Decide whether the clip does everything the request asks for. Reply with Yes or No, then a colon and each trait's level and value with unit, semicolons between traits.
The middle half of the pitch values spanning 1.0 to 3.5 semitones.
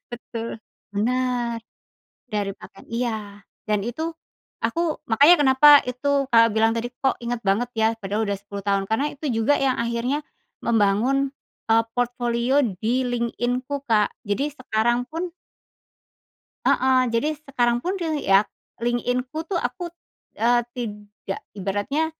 Yes: average, 3.2 semitones